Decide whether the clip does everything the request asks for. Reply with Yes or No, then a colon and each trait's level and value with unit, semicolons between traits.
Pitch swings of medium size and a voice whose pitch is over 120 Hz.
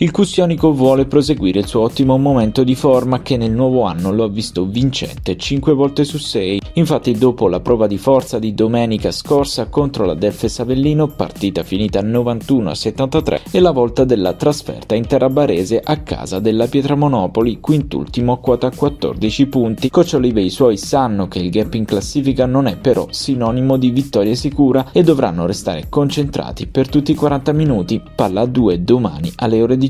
Yes: average, 4.3 semitones; low, 130 Hz